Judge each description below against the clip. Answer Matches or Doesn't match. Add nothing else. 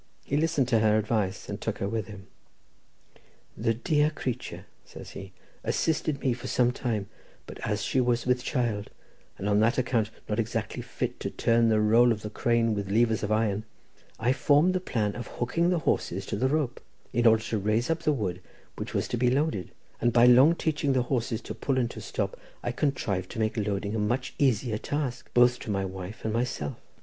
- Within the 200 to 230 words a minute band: Matches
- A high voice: Doesn't match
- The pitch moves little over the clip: Doesn't match